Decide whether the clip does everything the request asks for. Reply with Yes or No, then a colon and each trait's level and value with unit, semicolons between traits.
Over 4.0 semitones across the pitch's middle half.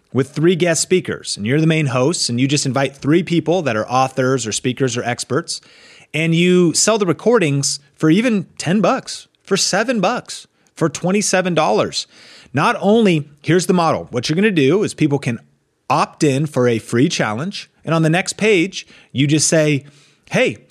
Yes: average, 4.7 semitones